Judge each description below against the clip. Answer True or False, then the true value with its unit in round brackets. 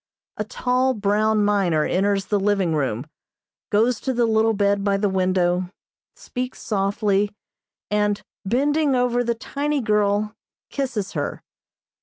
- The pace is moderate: False (130 wpm)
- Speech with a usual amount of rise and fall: True (3.3 semitones)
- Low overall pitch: False (210 Hz)